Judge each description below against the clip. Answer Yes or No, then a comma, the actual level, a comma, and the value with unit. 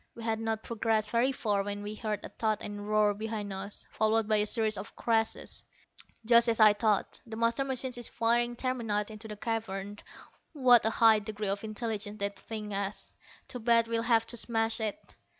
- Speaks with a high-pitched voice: Yes, high, 220 Hz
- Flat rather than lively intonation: Yes, narrow, 1.8 semitones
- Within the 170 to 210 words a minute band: Yes, average, 200 wpm